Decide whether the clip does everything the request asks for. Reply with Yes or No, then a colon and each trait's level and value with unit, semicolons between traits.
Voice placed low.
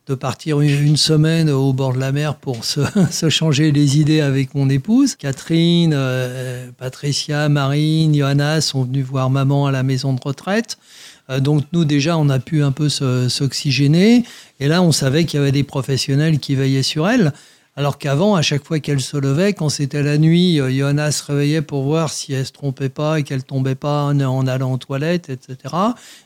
No: medium, 145 Hz